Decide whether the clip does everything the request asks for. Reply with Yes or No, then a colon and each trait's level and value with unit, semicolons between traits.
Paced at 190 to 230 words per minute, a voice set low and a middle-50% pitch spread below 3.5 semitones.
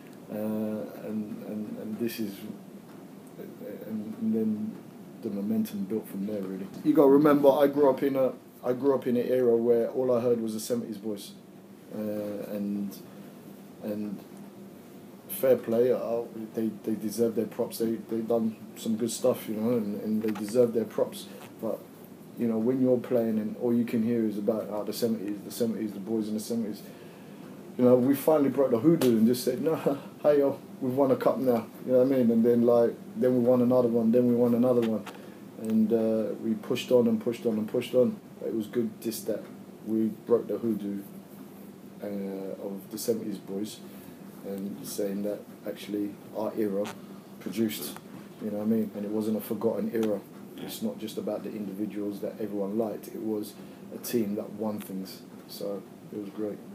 Yes: average, 195 wpm; low, 115 Hz; average, 2.8 semitones